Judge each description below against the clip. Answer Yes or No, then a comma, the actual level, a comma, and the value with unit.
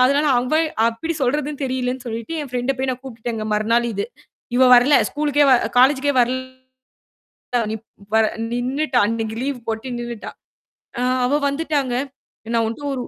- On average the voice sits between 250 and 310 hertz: Yes, very high, 255 Hz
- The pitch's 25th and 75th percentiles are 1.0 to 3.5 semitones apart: Yes, average, 3.2 semitones